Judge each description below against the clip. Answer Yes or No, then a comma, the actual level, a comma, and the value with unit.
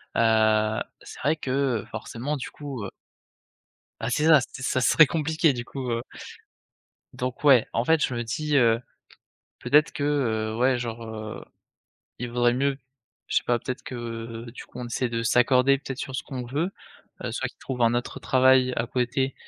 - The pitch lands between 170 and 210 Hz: No, low, 125 Hz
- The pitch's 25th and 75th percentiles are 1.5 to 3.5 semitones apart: Yes, average, 2.9 semitones